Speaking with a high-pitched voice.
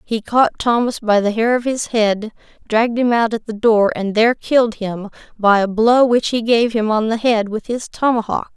Yes: high, 225 Hz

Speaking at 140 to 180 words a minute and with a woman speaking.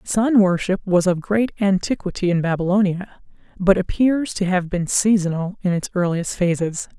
Yes: average, 155 wpm; female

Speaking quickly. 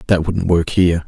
Yes: fast, 225 wpm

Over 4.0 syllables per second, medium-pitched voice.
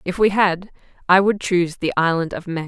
Yes: 5.4 syllables/s; medium, 180 Hz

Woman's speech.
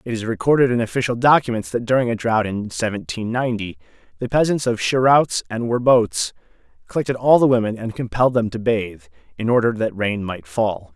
No: male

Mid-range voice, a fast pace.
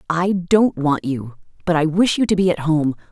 Yes: medium, 170 Hz; fast, 230 wpm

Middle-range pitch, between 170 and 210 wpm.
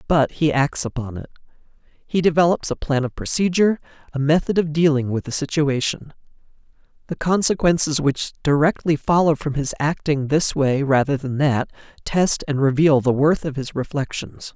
No: medium, 145 Hz; average, 160 wpm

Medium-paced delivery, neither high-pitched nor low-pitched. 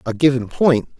No: average, 180 wpm; low, 130 Hz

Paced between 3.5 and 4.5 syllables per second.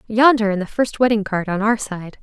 No: 5.4 syllables/s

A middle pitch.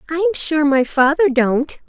No: very high, 295 Hz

